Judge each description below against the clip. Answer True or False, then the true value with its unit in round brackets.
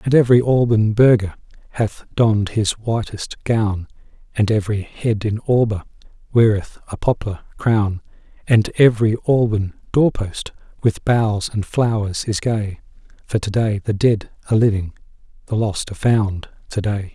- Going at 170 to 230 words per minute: False (145 wpm)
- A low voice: True (110 Hz)